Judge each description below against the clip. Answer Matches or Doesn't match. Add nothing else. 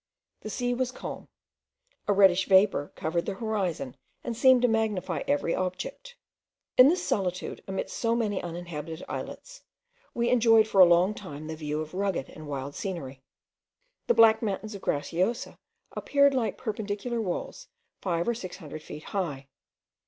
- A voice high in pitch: Matches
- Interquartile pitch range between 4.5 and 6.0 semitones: Matches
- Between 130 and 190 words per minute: Matches